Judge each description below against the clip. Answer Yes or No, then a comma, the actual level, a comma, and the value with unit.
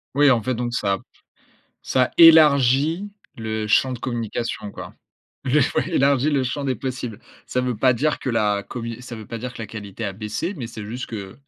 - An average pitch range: Yes, average, 3.4 semitones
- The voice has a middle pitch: No, low, 120 Hz